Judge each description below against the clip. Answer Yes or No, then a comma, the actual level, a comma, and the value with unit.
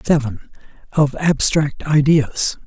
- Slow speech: Yes, slow, 90 wpm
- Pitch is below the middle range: No, medium, 150 Hz